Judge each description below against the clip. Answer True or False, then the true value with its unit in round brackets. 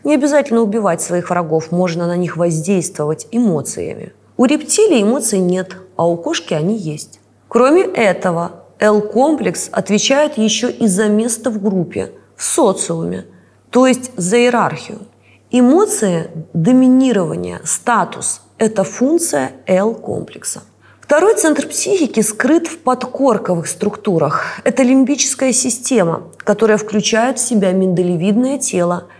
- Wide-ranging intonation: True (6.3 semitones)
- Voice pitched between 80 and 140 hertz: False (215 Hz)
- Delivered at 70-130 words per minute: True (115 wpm)